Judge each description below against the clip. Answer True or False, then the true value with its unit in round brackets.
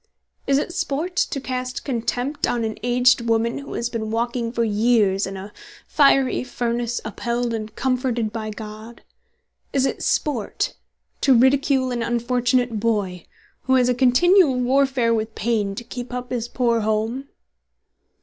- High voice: True (240 Hz)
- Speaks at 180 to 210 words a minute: False (150 wpm)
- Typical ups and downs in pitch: False (2.3 semitones)